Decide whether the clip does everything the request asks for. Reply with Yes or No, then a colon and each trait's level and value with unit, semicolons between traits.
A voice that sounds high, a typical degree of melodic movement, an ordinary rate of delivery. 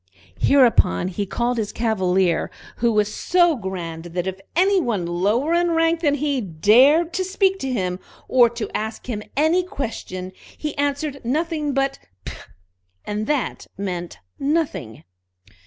No: high, 240 Hz; wide, 8.0 semitones; average, 145 wpm